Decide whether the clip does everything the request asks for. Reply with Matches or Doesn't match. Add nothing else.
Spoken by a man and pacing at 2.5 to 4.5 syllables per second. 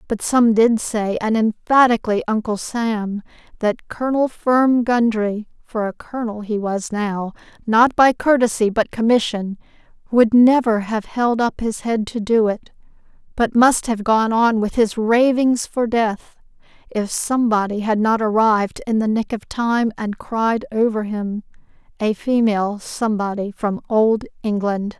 Doesn't match